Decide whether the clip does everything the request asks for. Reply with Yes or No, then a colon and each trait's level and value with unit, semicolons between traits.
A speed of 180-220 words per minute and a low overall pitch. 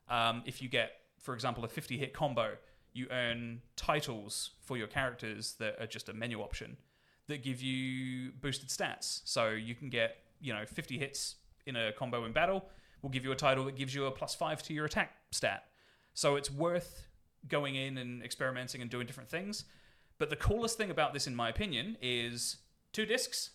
Yes: average, 200 wpm; low, 130 Hz